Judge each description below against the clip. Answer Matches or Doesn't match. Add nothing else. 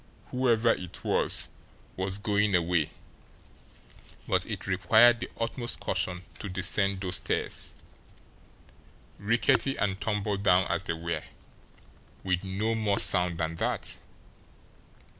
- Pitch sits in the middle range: Doesn't match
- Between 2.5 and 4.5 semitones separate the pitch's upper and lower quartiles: Matches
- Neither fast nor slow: Doesn't match